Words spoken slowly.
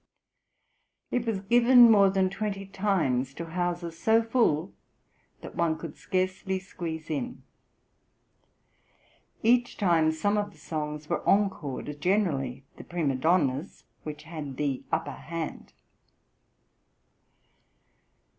Yes: slow, 110 wpm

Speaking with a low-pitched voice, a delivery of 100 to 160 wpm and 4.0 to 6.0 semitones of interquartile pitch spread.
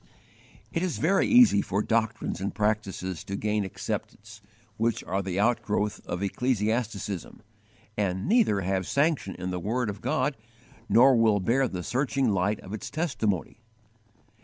Yes: low, 105 Hz; average, 150 wpm; average, 4.3 semitones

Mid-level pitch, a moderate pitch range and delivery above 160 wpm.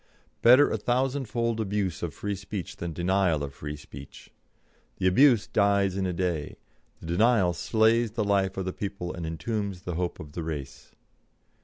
No: very low, 95 Hz; average, 4.1 semitones; average, 170 wpm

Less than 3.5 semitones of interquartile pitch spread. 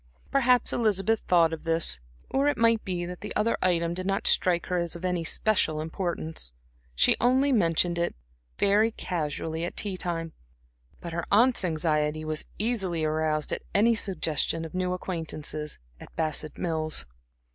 No: average, 4.0 semitones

